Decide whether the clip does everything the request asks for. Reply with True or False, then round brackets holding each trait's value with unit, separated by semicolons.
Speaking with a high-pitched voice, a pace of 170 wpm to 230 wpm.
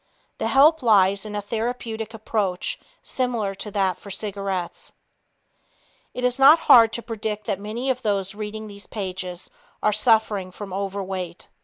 False (210 Hz; 150 wpm)